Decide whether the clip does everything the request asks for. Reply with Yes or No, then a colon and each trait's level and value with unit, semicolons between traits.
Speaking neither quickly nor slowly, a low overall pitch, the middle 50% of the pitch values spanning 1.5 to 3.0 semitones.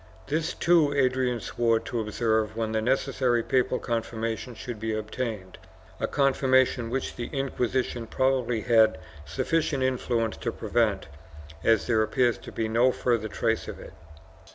Yes: average, 150 wpm; low, 120 Hz; narrow, 2.6 semitones